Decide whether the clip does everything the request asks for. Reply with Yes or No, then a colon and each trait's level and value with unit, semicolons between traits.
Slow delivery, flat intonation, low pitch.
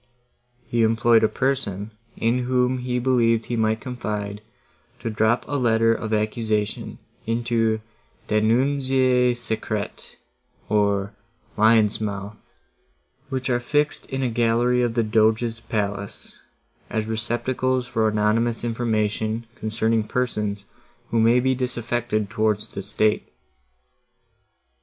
Yes: slow, 115 wpm; narrow, 2.3 semitones; low, 115 Hz